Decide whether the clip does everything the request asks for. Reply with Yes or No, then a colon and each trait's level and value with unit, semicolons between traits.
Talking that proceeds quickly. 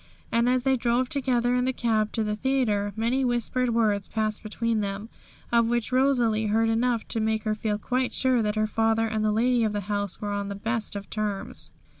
Yes: fast, 215 wpm